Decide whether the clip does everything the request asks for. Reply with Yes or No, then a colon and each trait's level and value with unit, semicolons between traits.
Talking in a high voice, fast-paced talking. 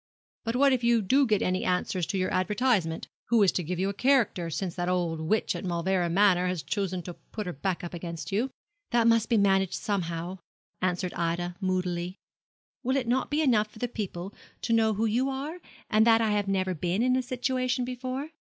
Yes: high, 200 Hz; fast, 210 wpm